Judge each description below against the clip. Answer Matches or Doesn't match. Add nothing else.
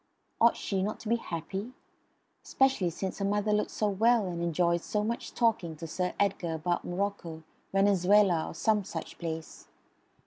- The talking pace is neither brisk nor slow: Matches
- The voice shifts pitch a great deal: Doesn't match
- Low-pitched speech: Doesn't match